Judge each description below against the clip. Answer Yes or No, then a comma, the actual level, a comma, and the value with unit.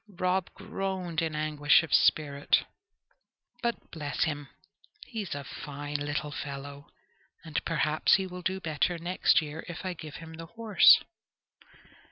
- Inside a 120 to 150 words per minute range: Yes, average, 140 wpm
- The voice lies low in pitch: No, medium, 160 Hz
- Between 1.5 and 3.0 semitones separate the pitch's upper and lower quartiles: No, average, 3.7 semitones